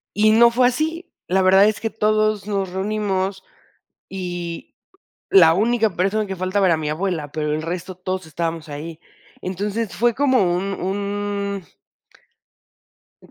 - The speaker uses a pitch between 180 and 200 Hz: Yes, high, 190 Hz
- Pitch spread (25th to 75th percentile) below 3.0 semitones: No, average, 3.6 semitones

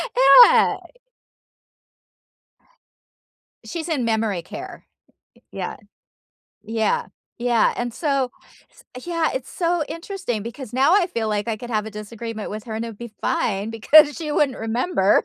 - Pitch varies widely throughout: Yes, wide, 6.0 semitones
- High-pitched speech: Yes, high, 240 Hz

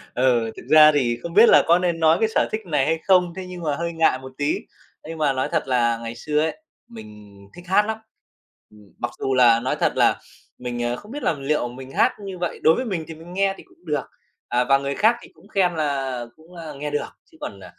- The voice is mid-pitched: Yes, medium, 150 Hz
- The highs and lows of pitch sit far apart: Yes, wide, 5.8 semitones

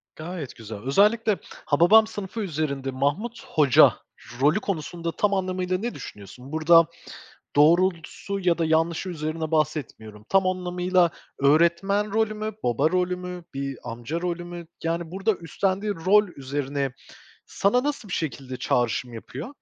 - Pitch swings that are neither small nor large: Yes, average, 5.0 semitones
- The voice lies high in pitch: No, medium, 170 Hz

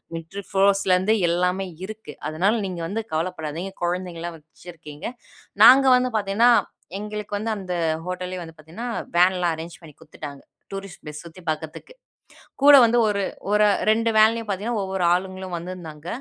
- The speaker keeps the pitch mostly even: No, average, 3.8 semitones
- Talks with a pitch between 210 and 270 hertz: No, medium, 185 Hz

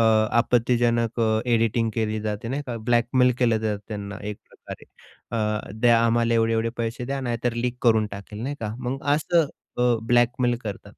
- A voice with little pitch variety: Yes, narrow, 1.8 semitones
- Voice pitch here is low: Yes, low, 115 Hz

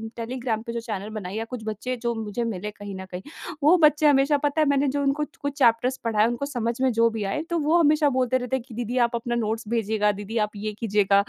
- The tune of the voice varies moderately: Yes, average, 4.0 semitones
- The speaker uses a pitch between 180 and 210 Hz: No, high, 235 Hz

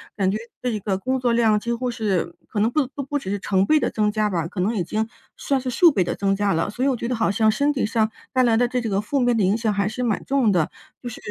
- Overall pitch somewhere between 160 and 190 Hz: No, high, 220 Hz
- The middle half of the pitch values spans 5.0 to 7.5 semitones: No, average, 3.7 semitones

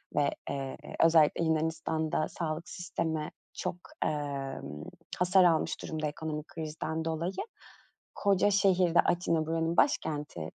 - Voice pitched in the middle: Yes, medium, 160 Hz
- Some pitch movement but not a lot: No, narrow, 1.9 semitones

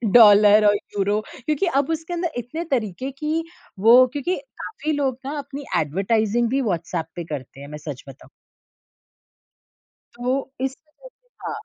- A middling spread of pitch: No, wide, 6.0 semitones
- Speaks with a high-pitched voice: Yes, high, 240 Hz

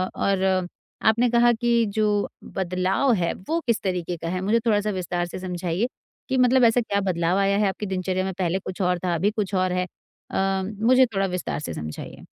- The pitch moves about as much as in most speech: Yes, average, 3.2 semitones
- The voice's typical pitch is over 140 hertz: Yes, high, 190 Hz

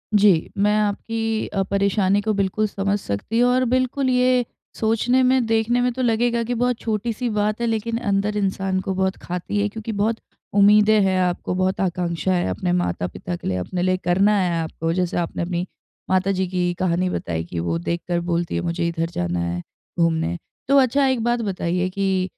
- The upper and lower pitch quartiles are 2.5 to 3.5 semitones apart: No, average, 4.2 semitones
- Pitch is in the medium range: No, high, 195 Hz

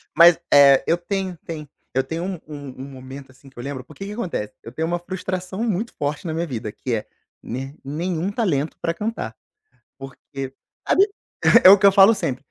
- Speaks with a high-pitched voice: No, medium, 160 Hz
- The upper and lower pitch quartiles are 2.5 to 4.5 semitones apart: No, wide, 5.6 semitones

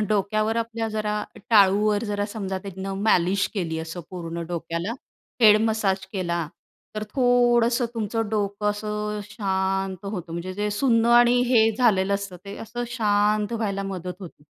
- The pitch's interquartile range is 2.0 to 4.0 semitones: Yes, narrow, 2.6 semitones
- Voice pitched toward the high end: Yes, high, 205 Hz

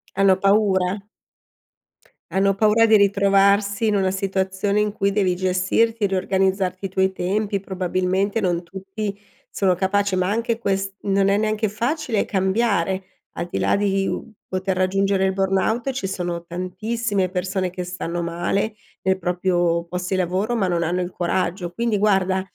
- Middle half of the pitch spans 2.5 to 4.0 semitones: No, narrow, 1.7 semitones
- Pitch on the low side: No, high, 195 Hz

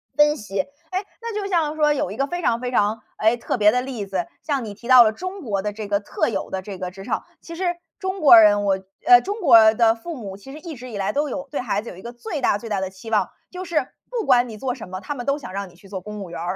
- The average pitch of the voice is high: Yes, high, 235 Hz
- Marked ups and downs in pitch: Yes, wide, 6.6 semitones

